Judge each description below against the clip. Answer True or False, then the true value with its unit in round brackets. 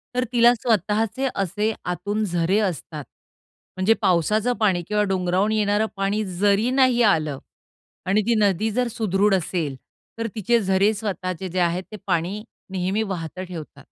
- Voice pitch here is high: True (200 Hz)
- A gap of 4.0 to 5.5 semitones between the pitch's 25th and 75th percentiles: False (3.1 semitones)